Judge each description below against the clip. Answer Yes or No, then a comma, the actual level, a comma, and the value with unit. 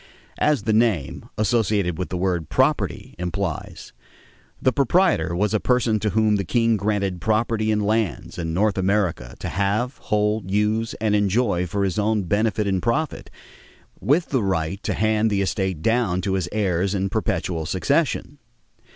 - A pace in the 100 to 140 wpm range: No, average, 160 wpm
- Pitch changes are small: No, average, 3.1 semitones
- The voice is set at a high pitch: No, low, 105 Hz